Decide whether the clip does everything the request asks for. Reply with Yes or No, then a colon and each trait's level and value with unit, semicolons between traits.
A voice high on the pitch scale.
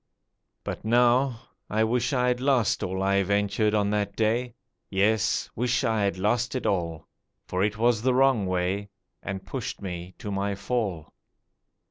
No: low, 105 Hz